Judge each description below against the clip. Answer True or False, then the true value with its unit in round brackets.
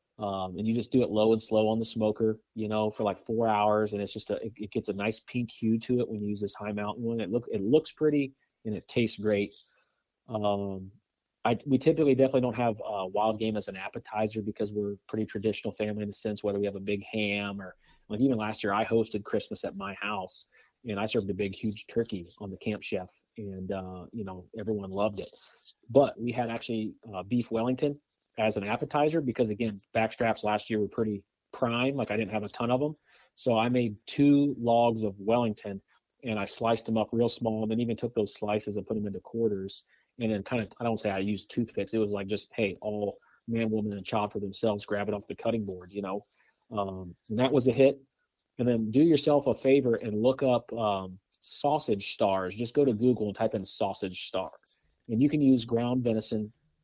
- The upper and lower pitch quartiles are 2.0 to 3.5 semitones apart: True (2.5 semitones)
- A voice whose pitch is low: True (110 Hz)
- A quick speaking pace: True (230 wpm)